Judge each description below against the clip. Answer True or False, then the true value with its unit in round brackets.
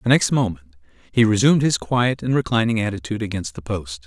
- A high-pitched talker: False (110 Hz)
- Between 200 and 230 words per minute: True (205 wpm)